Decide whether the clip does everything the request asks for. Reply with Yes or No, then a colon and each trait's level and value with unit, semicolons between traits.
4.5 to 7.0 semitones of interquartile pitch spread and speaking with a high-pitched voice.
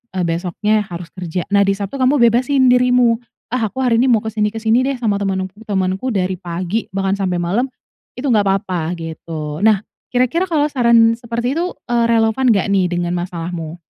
Yes: average, 4.9 semitones; high, 210 Hz